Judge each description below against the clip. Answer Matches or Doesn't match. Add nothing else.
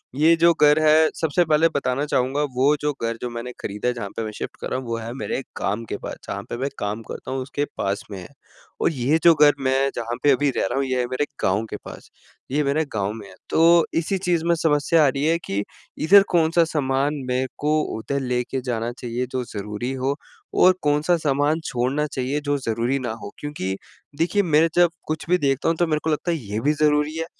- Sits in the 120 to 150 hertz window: Matches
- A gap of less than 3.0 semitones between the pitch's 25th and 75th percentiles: Doesn't match